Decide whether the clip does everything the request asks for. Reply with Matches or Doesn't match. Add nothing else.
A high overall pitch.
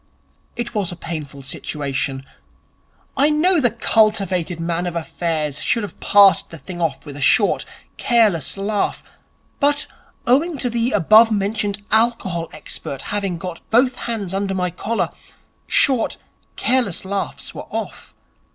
Matches